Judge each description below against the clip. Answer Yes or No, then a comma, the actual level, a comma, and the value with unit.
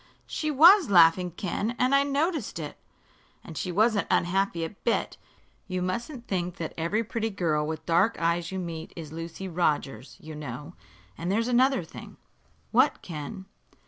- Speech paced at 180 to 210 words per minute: No, average, 155 wpm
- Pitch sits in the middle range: Yes, medium, 180 Hz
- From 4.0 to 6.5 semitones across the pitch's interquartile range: Yes, wide, 5.6 semitones